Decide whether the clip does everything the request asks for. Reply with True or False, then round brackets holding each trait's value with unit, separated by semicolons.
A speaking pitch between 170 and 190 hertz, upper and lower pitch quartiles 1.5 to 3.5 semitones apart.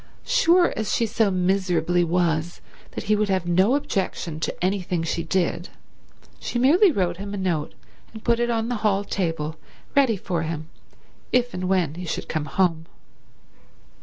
False (185 Hz; 4.4 semitones)